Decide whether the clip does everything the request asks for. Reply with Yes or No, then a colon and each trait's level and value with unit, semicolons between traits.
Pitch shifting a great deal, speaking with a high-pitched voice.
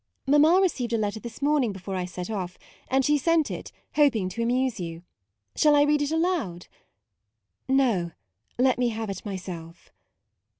Yes: wide, 7.8 semitones; high, 230 Hz